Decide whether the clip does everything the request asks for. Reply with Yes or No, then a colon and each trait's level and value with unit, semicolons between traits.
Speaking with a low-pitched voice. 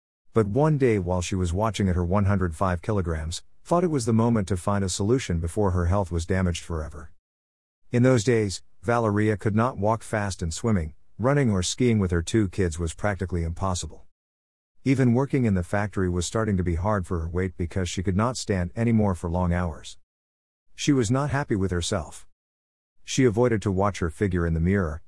Yes: very low, 95 Hz